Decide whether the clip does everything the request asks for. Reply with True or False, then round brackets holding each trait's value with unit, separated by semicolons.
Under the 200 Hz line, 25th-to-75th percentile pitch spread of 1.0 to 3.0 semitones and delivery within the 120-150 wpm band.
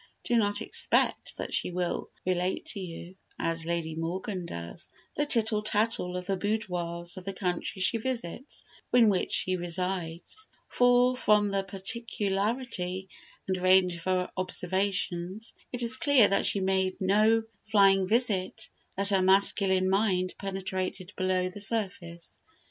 True (190 Hz; 2.7 semitones; 145 wpm)